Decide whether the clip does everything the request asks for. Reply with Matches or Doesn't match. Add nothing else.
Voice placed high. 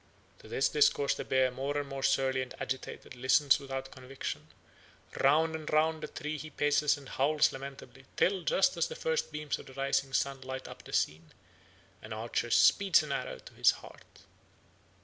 Doesn't match